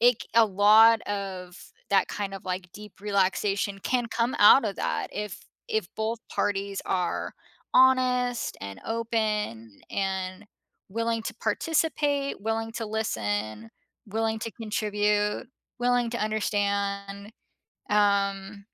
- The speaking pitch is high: Yes, high, 210 Hz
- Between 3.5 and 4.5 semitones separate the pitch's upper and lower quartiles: No, narrow, 2.5 semitones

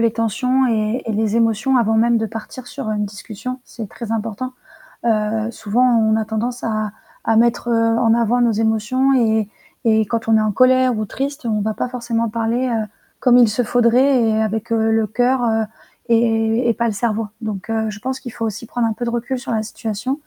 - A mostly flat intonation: Yes, narrow, 1.9 semitones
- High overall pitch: Yes, high, 225 Hz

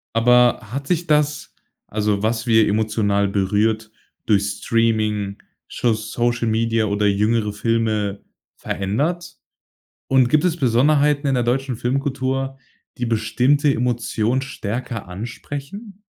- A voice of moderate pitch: No, low, 115 Hz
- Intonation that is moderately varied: Yes, average, 3.8 semitones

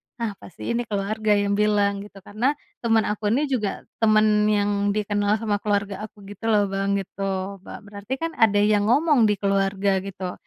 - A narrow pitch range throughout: Yes, narrow, 1.4 semitones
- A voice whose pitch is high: Yes, high, 205 Hz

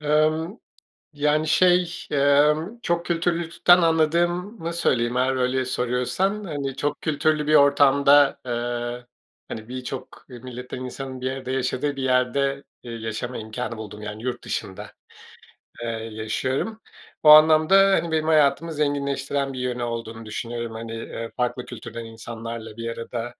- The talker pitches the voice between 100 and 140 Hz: Yes, low, 135 Hz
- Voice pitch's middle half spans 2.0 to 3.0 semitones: No, average, 4.5 semitones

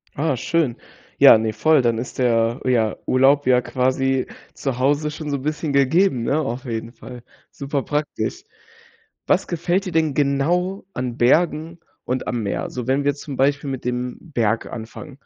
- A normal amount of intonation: Yes, average, 3.5 semitones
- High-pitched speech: No, low, 135 Hz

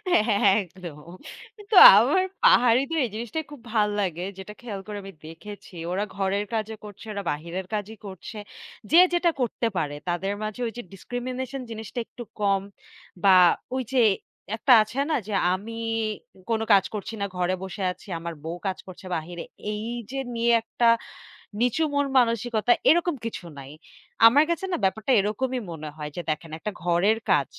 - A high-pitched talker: Yes, high, 210 Hz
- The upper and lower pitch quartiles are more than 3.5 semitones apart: Yes, average, 4.3 semitones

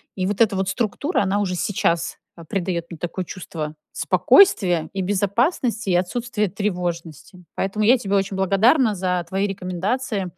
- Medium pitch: No, high, 195 Hz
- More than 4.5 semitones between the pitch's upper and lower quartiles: No, average, 2.8 semitones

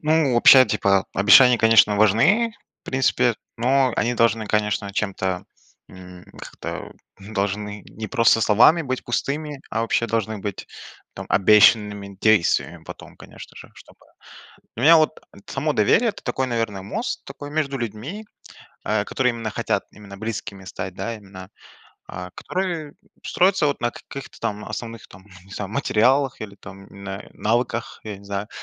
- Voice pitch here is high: No, low, 110 Hz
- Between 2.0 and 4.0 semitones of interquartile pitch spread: No, average, 4.7 semitones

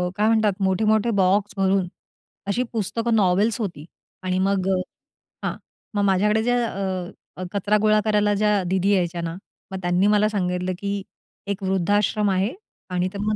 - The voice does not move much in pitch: Yes, narrow, 2.3 semitones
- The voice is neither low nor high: No, high, 200 Hz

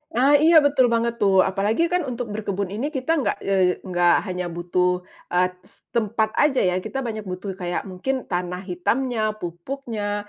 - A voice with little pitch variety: No, wide, 5.5 semitones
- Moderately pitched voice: No, high, 205 Hz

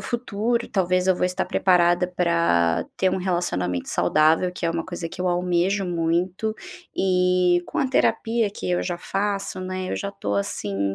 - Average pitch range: No, narrow, 2.1 semitones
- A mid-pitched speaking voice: Yes, medium, 180 Hz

